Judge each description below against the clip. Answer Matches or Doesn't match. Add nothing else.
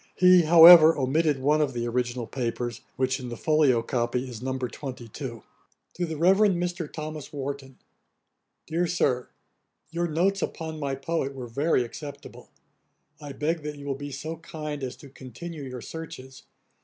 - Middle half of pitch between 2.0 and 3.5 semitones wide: Doesn't match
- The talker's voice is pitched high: Doesn't match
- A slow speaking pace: Doesn't match